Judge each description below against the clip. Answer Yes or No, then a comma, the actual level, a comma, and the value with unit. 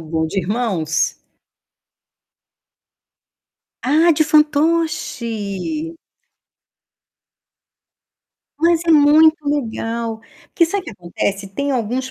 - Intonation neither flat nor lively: No, wide, 7.6 semitones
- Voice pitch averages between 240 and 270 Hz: Yes, very high, 260 Hz